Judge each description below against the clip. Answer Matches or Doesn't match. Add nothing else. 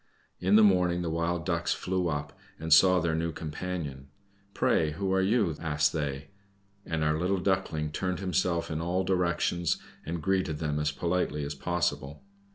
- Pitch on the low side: Matches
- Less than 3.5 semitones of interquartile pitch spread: Matches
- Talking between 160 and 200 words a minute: Matches